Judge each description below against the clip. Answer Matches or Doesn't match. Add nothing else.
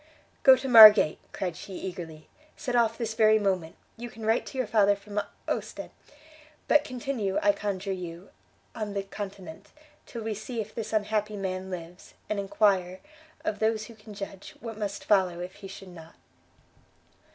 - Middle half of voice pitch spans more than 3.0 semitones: Doesn't match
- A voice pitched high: Matches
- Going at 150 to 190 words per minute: Matches